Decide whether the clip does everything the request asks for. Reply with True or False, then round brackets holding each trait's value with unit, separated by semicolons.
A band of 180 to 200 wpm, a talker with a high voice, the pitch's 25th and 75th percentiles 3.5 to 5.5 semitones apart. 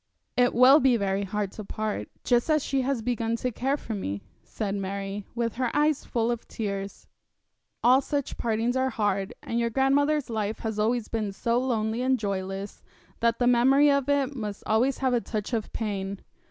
True (185 wpm; 230 Hz; 3.8 semitones)